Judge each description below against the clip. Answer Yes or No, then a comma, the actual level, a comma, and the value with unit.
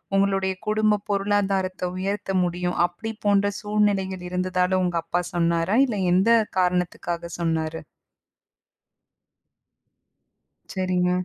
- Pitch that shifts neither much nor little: No, narrow, 2.0 semitones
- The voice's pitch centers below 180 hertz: No, medium, 185 Hz